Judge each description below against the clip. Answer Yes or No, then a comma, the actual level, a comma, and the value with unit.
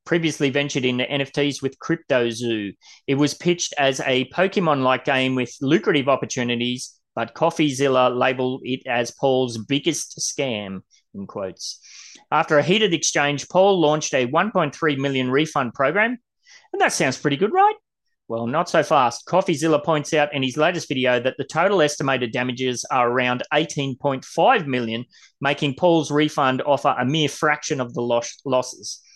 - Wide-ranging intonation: No, average, 3.8 semitones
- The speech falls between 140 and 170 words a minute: Yes, average, 150 wpm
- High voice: No, medium, 140 Hz